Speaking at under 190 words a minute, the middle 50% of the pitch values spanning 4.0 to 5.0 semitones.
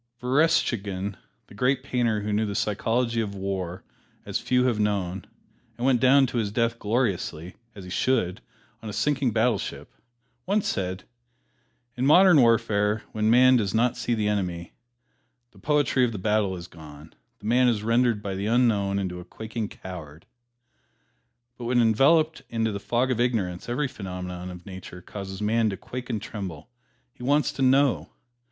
Yes: average, 170 wpm; average, 4.3 semitones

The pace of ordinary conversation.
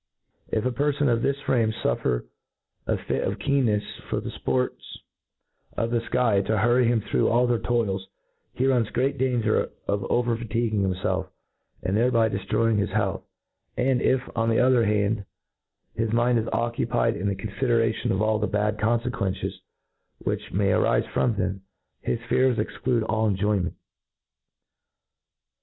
Yes: average, 155 wpm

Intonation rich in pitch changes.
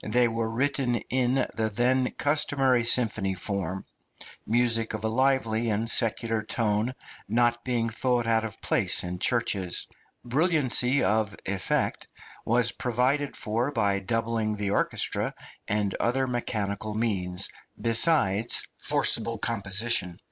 No: average, 2.7 semitones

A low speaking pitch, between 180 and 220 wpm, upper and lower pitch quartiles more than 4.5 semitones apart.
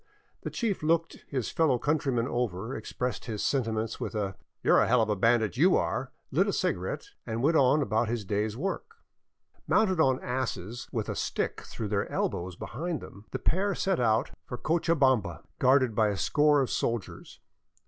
Yes: low, 125 Hz; average, 190 wpm; wide, 5.5 semitones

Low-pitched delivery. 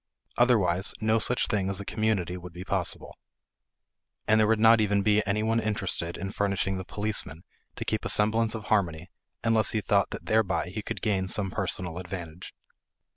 Yes: low, 100 Hz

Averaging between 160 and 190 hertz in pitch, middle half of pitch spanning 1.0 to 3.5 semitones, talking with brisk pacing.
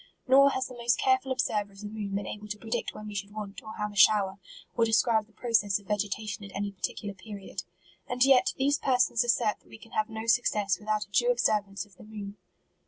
No: high, 215 Hz; average, 2.7 semitones; fast, 230 wpm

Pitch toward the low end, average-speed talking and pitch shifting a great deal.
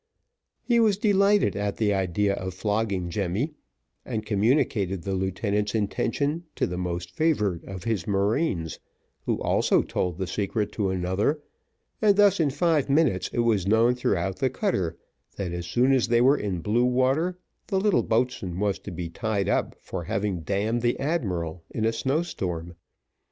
Yes: low, 105 Hz; average, 165 wpm; wide, 6.0 semitones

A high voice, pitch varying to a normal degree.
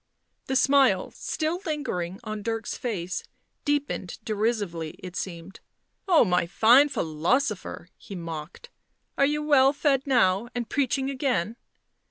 No: high, 230 Hz; wide, 7.2 semitones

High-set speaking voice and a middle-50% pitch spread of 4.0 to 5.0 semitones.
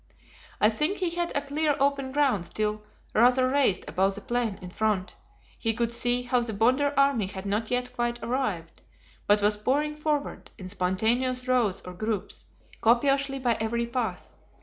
Yes: high, 240 Hz; average, 4.4 semitones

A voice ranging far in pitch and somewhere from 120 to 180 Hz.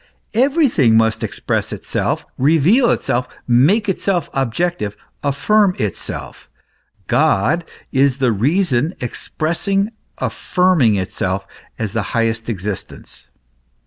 Yes: wide, 8.5 semitones; low, 135 Hz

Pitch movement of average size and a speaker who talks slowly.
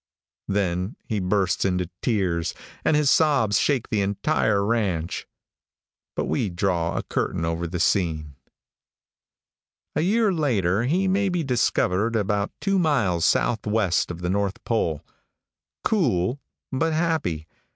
No: wide, 8.0 semitones; slow, 130 wpm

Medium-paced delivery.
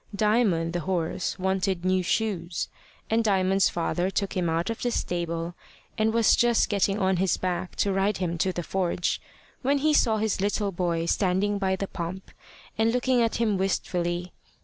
Yes: average, 175 wpm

